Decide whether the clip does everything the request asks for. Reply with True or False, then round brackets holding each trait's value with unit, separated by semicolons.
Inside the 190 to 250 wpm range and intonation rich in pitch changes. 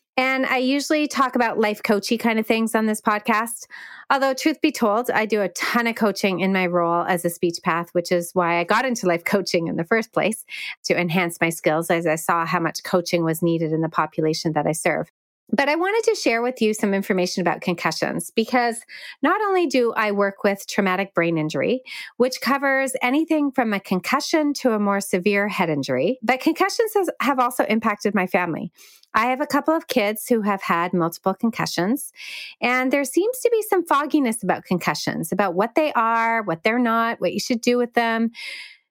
True (205 wpm; 6.3 semitones)